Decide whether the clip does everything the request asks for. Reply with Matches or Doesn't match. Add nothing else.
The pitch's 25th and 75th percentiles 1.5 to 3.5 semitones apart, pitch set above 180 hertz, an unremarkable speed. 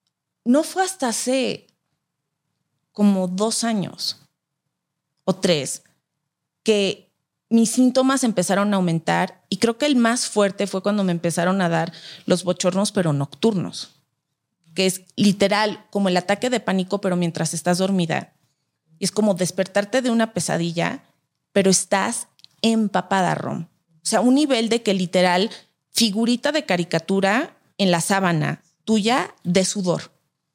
Doesn't match